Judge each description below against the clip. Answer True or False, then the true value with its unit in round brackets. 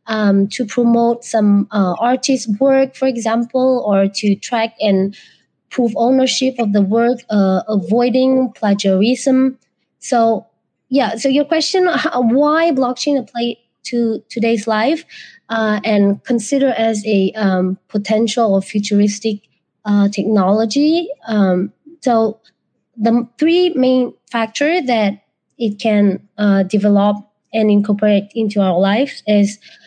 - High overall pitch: True (225 Hz)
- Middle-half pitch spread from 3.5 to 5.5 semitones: True (3.9 semitones)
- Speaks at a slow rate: True (125 wpm)